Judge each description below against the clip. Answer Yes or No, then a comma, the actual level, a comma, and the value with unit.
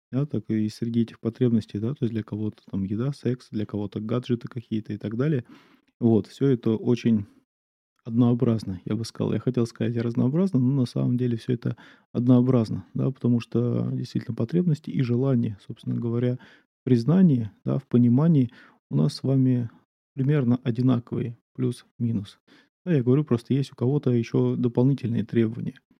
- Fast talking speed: Yes, fast, 165 wpm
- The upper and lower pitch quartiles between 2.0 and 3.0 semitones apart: Yes, narrow, 2.5 semitones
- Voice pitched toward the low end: Yes, low, 120 Hz